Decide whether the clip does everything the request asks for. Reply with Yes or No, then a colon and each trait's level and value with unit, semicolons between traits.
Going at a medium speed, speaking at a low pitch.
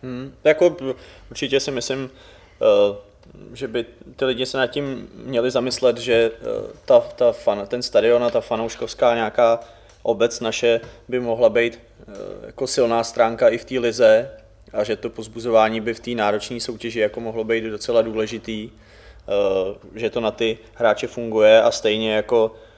Yes: average, 135 wpm; low, 115 Hz